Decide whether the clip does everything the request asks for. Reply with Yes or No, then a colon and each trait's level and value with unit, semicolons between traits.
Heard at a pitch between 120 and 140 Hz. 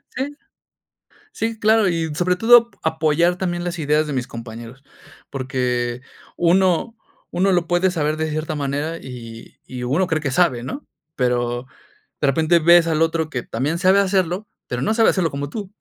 No: medium, 160 Hz